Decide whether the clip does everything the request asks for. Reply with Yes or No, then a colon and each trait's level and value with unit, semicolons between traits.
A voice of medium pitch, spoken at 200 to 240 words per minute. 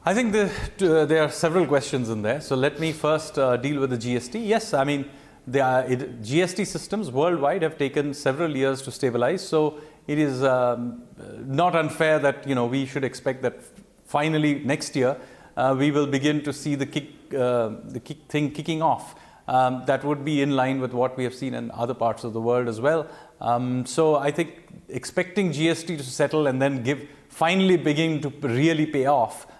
Yes: medium, 145 Hz; fast, 205 wpm